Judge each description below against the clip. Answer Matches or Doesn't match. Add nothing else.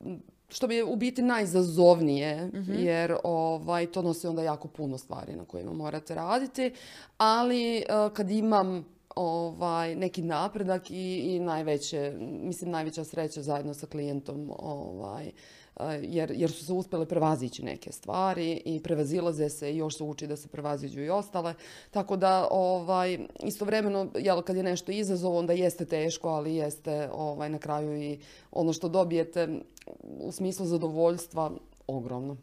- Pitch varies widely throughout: Doesn't match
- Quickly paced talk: Doesn't match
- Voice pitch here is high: Doesn't match